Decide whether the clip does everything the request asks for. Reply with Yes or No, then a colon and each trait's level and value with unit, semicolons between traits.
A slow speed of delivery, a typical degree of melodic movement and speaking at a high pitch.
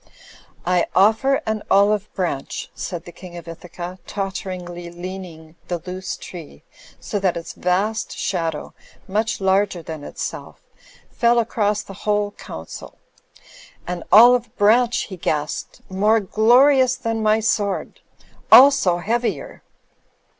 Yes: slow, 125 wpm; average, 3.9 semitones; high, 195 Hz